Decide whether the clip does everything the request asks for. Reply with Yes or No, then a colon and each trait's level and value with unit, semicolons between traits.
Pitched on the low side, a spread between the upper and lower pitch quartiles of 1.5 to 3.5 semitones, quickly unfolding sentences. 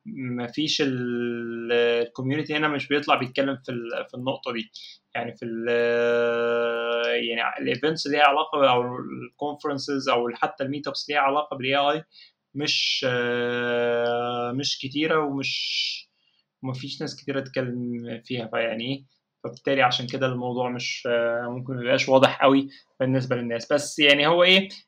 Yes: low, 130 Hz; average, 3.2 semitones; fast, 140 wpm